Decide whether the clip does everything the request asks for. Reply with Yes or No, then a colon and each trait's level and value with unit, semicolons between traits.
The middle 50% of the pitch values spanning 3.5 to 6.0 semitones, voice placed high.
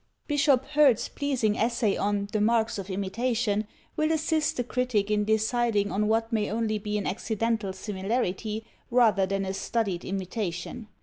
No: average, 2.9 semitones; high, 220 Hz